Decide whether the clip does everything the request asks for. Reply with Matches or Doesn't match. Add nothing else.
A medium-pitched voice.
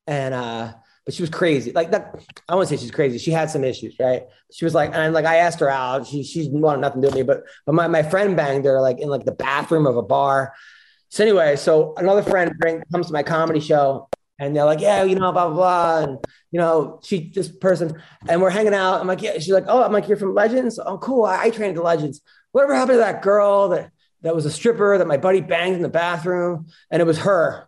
Matches